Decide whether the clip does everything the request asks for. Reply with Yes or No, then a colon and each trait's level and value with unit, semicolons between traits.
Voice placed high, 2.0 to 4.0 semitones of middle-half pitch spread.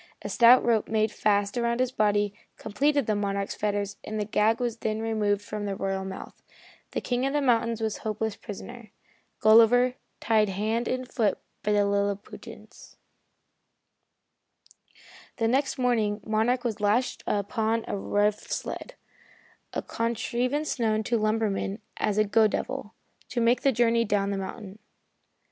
Yes: high, 220 Hz; narrow, 2.5 semitones